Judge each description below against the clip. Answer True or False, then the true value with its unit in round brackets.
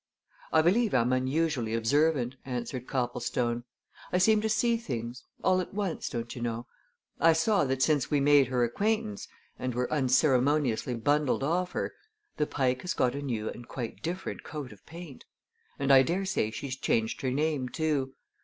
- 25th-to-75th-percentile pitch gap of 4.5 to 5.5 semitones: True (4.8 semitones)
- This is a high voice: False (135 Hz)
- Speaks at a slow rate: False (170 wpm)